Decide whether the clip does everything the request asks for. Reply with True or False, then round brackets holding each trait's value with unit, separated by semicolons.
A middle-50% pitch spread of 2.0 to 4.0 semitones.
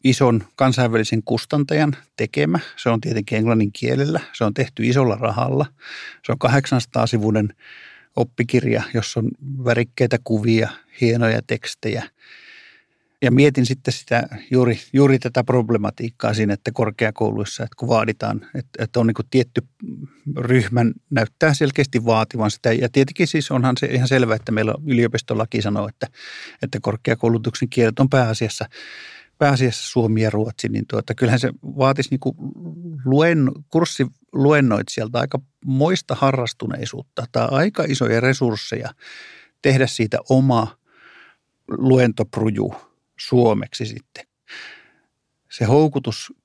True (2.9 semitones)